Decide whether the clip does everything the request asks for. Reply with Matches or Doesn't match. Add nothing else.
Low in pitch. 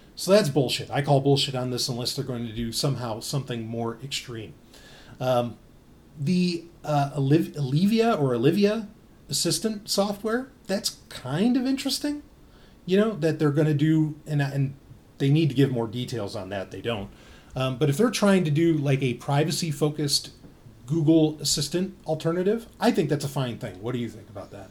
Doesn't match